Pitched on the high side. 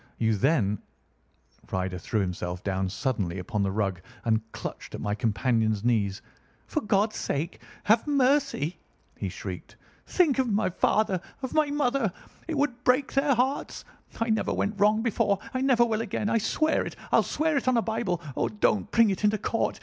Yes: high, 210 Hz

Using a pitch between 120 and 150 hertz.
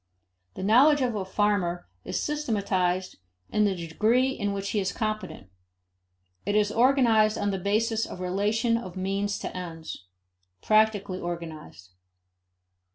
No: high, 205 Hz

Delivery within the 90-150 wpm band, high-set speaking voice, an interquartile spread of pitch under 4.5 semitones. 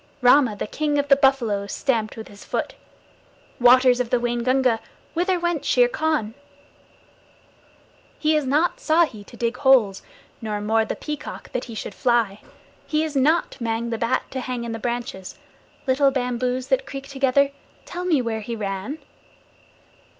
No: average, 160 wpm; very high, 250 Hz; average, 3.6 semitones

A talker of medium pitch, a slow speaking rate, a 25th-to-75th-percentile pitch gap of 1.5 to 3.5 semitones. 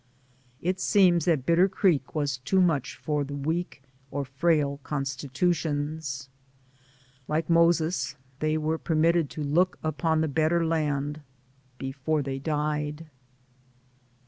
Yes: medium, 155 Hz; slow, 120 wpm; average, 2.8 semitones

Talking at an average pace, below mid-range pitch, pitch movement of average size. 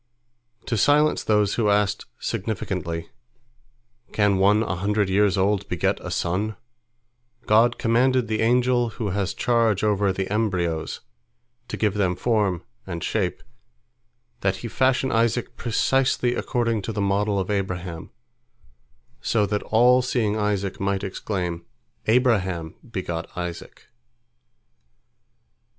No: slow, 120 wpm; low, 105 Hz; average, 3.3 semitones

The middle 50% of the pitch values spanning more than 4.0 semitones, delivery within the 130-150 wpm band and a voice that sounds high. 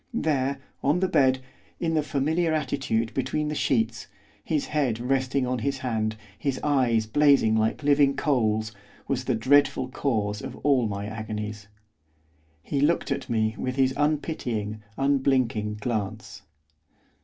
No: average, 4.4 semitones; average, 140 wpm; low, 130 Hz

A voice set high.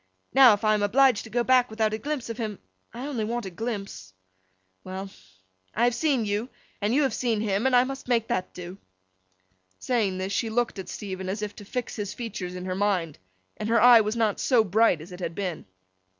Yes: high, 215 Hz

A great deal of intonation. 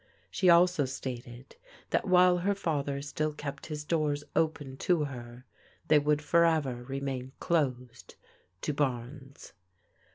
No: average, 3.4 semitones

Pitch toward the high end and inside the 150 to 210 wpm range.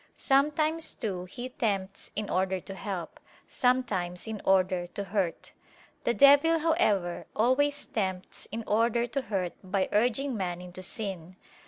No: high, 210 Hz; average, 140 wpm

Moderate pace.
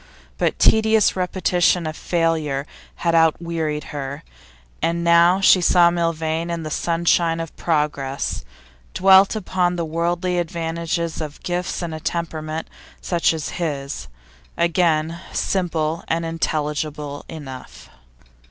No: slow, 115 wpm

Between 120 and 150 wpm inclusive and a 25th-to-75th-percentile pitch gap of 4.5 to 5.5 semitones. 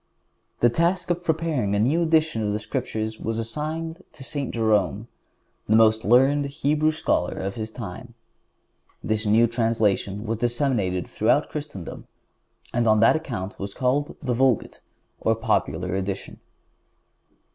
Yes: average, 140 wpm; average, 5.2 semitones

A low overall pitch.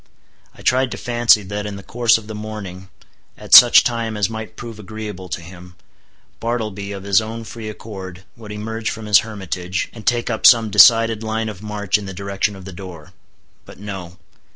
Yes: low, 105 Hz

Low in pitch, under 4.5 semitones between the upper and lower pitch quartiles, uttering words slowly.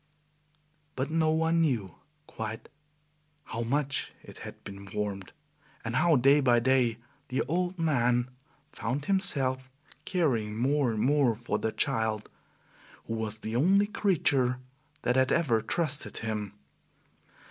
No: low, 130 Hz; average, 5.0 semitones; slow, 130 wpm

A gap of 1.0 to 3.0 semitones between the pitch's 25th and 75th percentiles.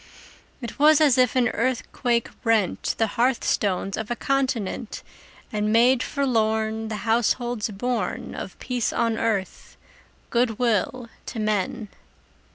Yes: narrow, 2.5 semitones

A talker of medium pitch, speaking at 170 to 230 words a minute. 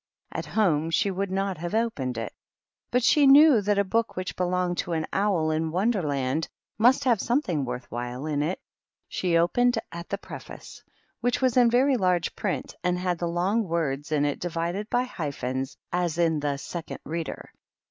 Yes: medium, 175 Hz; average, 185 wpm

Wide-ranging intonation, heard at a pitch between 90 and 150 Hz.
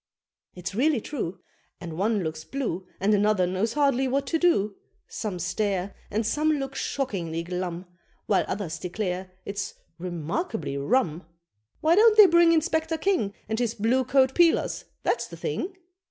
No: wide, 7.7 semitones; high, 215 Hz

